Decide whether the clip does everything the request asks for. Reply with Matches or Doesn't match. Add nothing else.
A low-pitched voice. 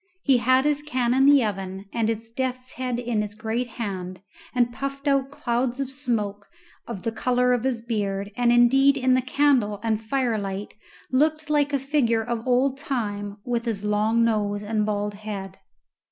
Doesn't match